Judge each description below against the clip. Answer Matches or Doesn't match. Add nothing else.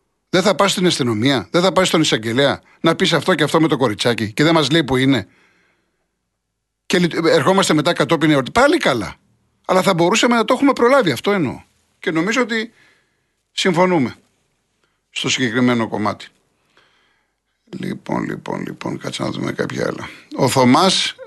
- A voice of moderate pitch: Matches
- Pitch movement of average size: Doesn't match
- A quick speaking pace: Doesn't match